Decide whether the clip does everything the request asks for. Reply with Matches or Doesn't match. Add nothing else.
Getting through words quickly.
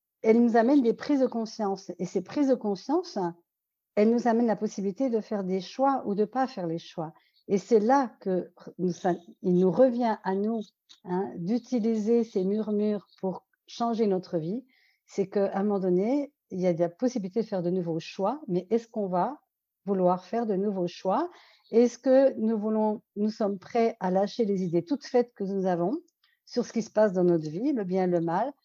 Doesn't match